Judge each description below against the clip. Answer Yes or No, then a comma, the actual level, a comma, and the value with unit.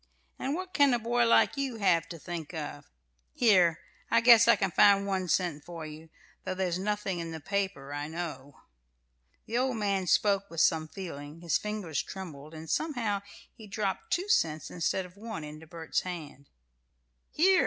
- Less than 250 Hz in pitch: Yes, medium, 185 Hz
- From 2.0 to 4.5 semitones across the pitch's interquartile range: No, average, 5.0 semitones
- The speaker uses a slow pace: No, average, 175 wpm